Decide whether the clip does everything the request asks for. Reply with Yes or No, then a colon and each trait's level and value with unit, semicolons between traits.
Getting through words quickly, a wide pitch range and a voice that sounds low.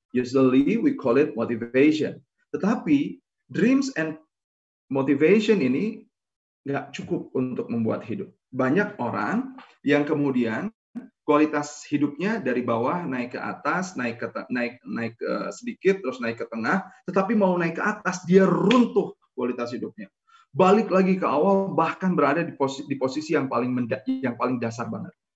No: fast, 150 wpm; wide, 7.4 semitones; medium, 155 Hz